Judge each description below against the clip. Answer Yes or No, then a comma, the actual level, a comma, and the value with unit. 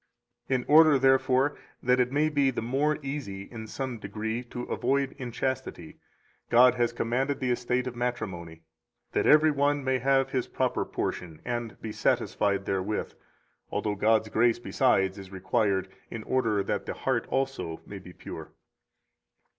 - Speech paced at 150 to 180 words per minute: Yes, average, 155 wpm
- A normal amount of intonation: Yes, average, 4.0 semitones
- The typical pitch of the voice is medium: No, low, 120 Hz